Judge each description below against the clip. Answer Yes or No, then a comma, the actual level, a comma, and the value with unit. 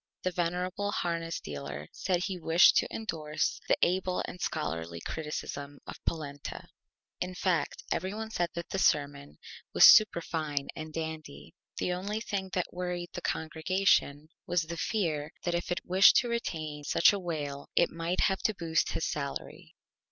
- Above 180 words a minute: No, average, 160 wpm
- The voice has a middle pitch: Yes, medium, 170 Hz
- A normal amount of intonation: Yes, average, 3.4 semitones